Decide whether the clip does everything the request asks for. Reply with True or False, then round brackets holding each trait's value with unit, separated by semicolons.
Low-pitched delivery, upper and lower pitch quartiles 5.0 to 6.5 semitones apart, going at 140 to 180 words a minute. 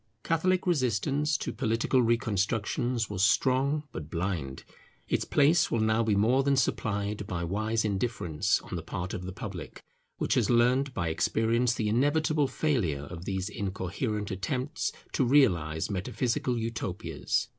True (110 Hz; 5.3 semitones; 145 wpm)